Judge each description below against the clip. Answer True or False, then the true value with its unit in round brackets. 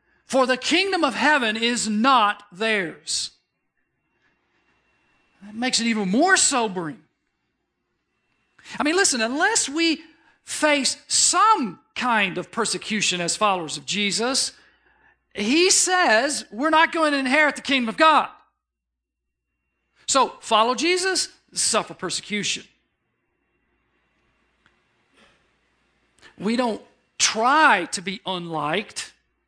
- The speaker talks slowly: True (100 wpm)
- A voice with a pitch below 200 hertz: False (235 Hz)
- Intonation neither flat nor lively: False (7.4 semitones)